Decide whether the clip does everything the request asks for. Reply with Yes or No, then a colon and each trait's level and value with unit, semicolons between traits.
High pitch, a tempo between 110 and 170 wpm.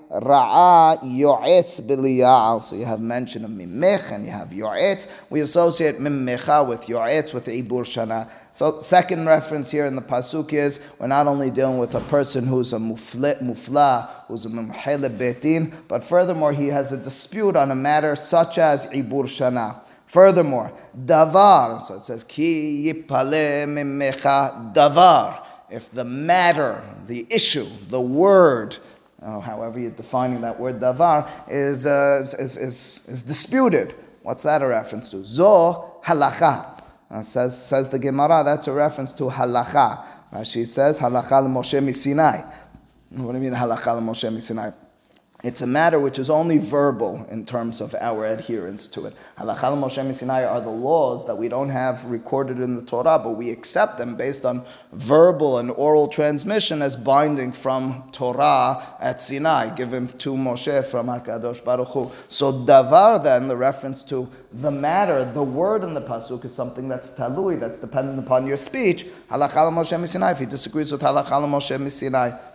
No: low, 135 Hz; average, 160 wpm